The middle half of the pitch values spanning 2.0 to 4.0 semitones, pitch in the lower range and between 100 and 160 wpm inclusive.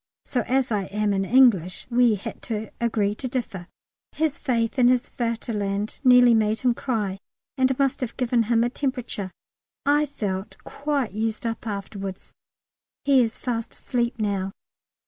No: average, 3.5 semitones; high, 230 Hz; average, 155 wpm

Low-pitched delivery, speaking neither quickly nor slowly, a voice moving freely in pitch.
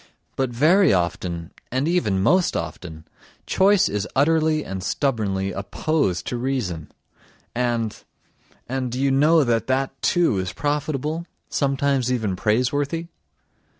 No: low, 130 Hz; slow, 120 wpm; wide, 7.1 semitones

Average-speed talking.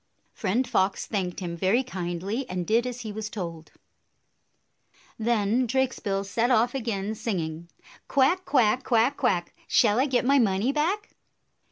Yes: average, 145 wpm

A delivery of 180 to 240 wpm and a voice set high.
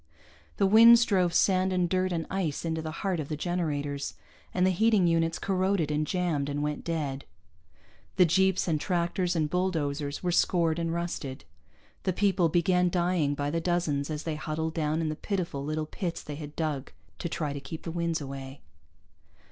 No: average, 185 wpm; medium, 165 Hz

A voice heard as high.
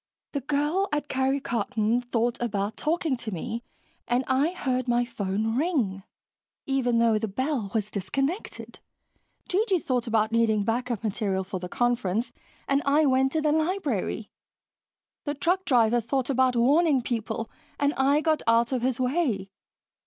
Yes: high, 245 Hz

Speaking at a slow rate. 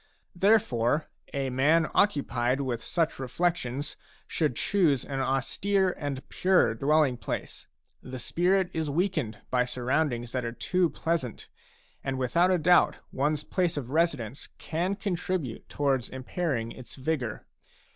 Yes: slow, 130 wpm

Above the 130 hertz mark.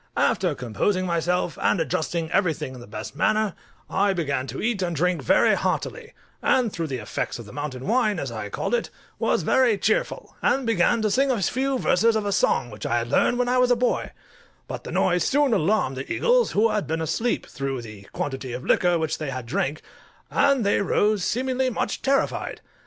Yes: medium, 185 Hz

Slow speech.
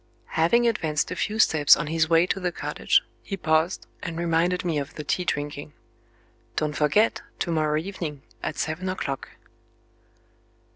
No: average, 155 wpm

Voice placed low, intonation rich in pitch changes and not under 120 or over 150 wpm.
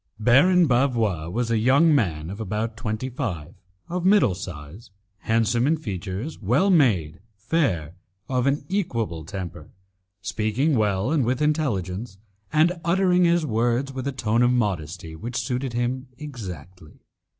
Yes: low, 120 Hz; wide, 6.7 semitones; average, 140 wpm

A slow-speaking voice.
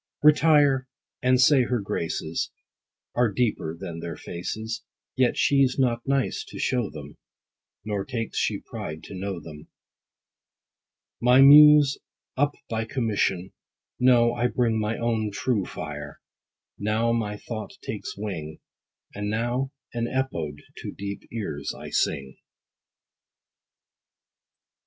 Yes: slow, 120 wpm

